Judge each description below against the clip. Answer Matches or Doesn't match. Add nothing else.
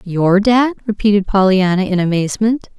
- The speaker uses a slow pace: Matches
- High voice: Matches